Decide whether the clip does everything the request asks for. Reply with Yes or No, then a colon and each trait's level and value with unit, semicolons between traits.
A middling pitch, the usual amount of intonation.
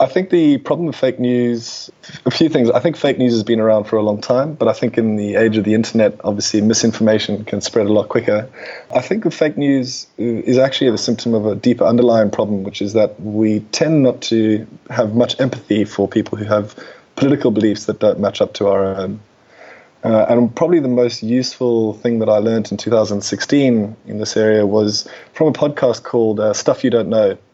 No: low, 115 Hz; average, 3.0 semitones